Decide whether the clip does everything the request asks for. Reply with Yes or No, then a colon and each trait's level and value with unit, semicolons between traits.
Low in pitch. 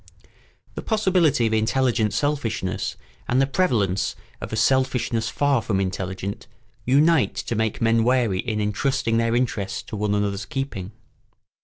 Yes: low, 115 Hz